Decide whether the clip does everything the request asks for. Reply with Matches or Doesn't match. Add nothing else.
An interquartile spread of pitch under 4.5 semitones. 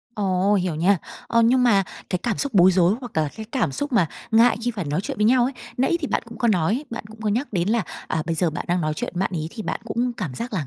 Doesn't match